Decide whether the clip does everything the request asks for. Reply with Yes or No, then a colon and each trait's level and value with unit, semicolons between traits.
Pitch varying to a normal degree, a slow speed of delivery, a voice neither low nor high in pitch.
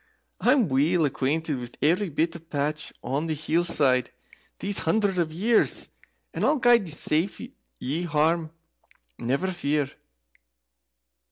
Yes: average, 3.5 semitones; slow, 120 wpm; medium, 160 Hz